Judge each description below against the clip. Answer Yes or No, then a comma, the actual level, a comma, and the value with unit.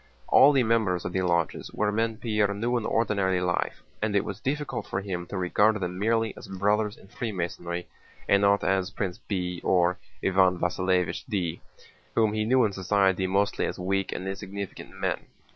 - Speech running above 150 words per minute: Yes, average, 180 wpm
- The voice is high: No, low, 100 Hz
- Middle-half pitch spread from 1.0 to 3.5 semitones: Yes, average, 2.9 semitones